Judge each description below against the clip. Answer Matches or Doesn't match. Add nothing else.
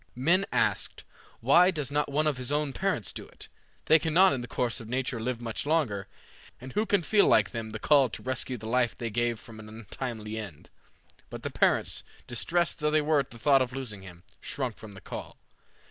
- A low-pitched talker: Matches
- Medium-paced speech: Doesn't match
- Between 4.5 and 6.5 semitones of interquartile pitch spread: Matches